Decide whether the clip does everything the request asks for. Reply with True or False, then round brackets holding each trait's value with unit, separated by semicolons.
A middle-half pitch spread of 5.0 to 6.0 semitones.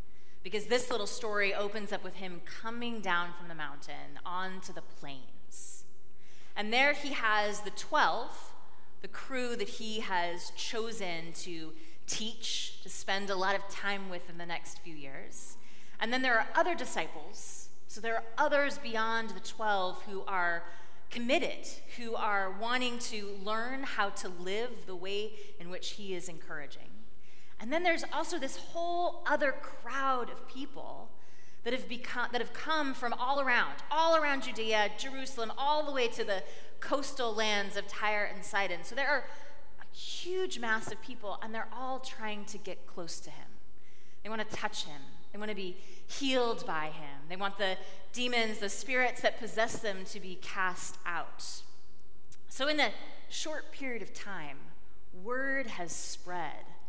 True (5.3 semitones)